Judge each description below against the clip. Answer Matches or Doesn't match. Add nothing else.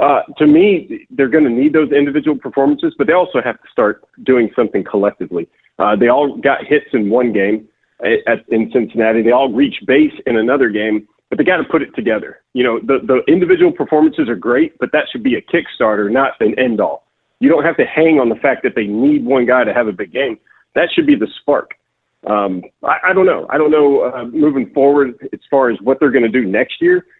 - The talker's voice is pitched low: Doesn't match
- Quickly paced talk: Matches